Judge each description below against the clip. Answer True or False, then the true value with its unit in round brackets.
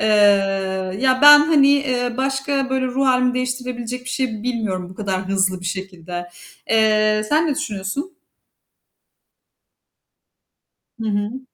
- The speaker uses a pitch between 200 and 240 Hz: False (250 Hz)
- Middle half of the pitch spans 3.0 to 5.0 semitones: True (4.7 semitones)